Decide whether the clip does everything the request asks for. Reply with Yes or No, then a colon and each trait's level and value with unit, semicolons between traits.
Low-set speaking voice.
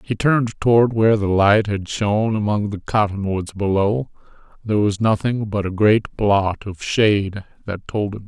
Yes: low, 105 Hz